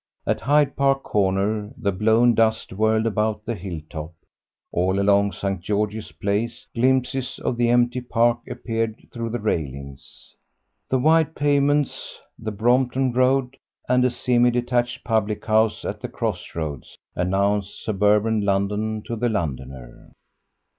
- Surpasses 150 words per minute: No, average, 140 wpm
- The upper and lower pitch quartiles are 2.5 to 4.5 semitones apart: Yes, average, 3.6 semitones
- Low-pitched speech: Yes, low, 110 Hz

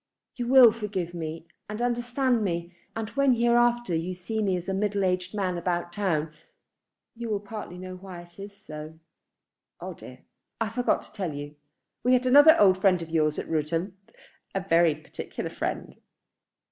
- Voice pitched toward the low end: No, high, 190 Hz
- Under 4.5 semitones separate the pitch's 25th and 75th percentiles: No, average, 4.9 semitones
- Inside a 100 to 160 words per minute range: No, average, 170 wpm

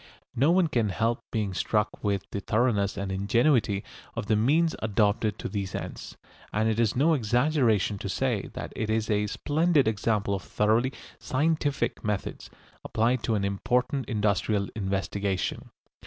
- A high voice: No, low, 110 Hz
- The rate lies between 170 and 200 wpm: No, average, 155 wpm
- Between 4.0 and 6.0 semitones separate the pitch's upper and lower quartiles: No, average, 3.6 semitones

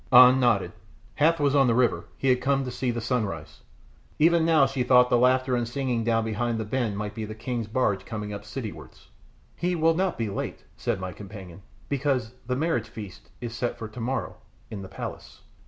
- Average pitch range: Yes, average, 3.5 semitones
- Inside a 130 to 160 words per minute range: No, fast, 205 wpm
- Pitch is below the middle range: Yes, low, 120 Hz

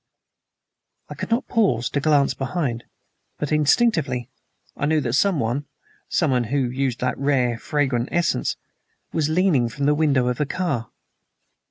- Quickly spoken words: No, average, 145 wpm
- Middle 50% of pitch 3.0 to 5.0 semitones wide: Yes, average, 4.1 semitones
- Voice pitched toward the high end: No, medium, 140 Hz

